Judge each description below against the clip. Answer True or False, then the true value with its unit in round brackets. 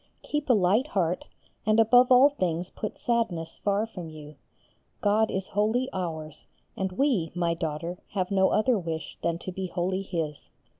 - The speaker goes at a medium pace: True (165 wpm)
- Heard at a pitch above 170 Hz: True (190 Hz)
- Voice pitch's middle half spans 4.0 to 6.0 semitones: True (4.7 semitones)